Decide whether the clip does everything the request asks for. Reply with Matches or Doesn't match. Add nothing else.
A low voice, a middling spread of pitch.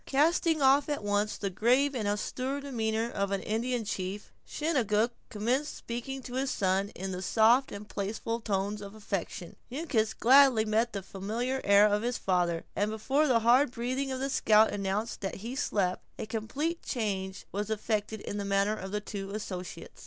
Doesn't match